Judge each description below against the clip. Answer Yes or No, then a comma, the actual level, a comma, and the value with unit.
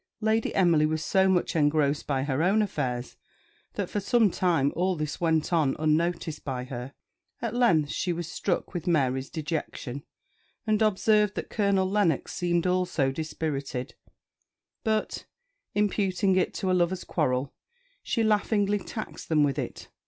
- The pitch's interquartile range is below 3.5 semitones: No, average, 5.1 semitones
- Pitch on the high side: No, medium, 170 Hz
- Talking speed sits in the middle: Yes, average, 150 wpm